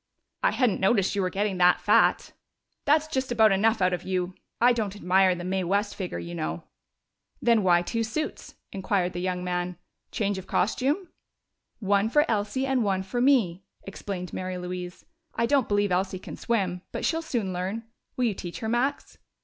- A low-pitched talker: No, high, 195 Hz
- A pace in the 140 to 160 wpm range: No, average, 185 wpm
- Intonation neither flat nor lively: Yes, average, 4.2 semitones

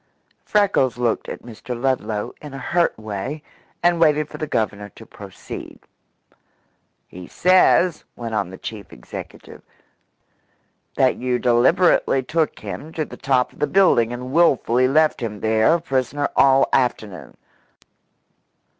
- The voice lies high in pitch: No, low, 130 Hz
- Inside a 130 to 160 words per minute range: Yes, slow, 135 wpm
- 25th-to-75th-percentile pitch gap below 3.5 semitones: No, wide, 5.4 semitones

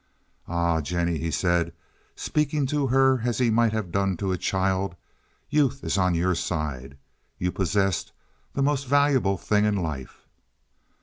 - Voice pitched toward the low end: Yes, very low, 95 Hz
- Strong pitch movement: Yes, wide, 6.9 semitones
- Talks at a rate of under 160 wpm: Yes, average, 150 wpm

